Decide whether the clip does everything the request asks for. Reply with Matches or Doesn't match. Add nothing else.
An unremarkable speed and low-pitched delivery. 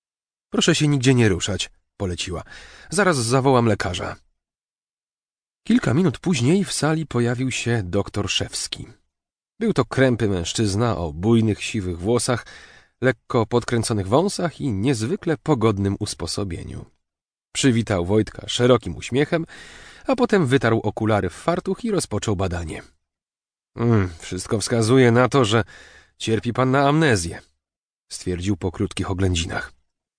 Matches